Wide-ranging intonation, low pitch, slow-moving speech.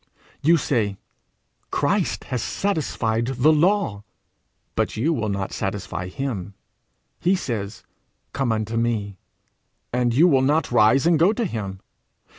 Yes: wide, 6.7 semitones; low, 120 Hz; slow, 130 wpm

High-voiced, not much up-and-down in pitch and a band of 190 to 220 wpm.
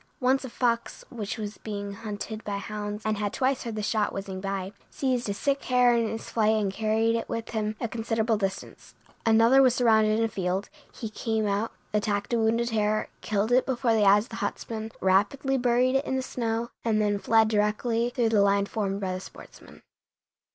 Yes: high, 220 Hz; narrow, 2.3 semitones; fast, 205 wpm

